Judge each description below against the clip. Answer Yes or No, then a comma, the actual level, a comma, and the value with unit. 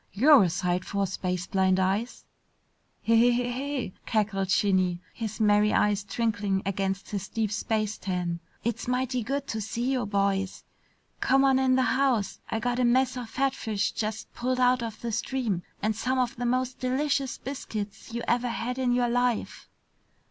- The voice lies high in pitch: Yes, high, 230 Hz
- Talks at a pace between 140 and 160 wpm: No, average, 170 wpm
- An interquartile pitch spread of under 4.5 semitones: Yes, average, 4.0 semitones